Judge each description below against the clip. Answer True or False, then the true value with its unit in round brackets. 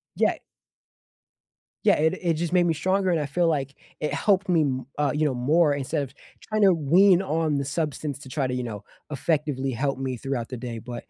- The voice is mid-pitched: True (145 Hz)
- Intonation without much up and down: False (4.2 semitones)